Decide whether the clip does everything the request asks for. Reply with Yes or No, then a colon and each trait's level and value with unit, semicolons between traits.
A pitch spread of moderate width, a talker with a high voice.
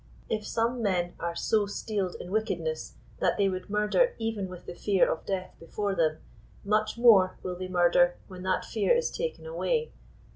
Yes: average, 3.6 semitones; high, 200 Hz